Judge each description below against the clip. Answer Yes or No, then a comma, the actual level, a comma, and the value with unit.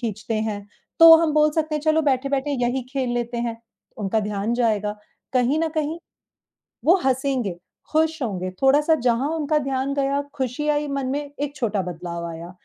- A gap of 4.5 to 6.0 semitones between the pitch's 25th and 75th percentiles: Yes, average, 5.2 semitones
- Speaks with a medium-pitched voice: No, very high, 265 Hz